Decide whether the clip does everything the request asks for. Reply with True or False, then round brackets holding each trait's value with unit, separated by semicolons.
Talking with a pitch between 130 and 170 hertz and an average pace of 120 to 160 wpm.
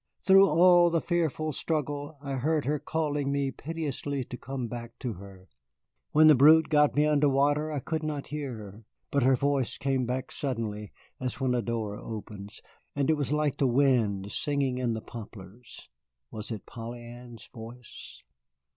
False (135 Hz; 175 wpm)